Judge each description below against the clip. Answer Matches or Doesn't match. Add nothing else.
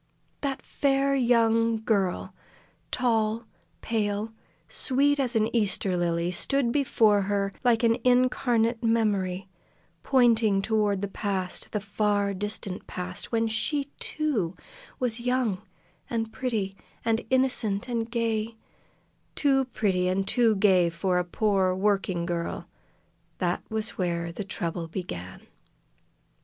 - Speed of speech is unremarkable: Doesn't match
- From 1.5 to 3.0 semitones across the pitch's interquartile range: Doesn't match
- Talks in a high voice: Matches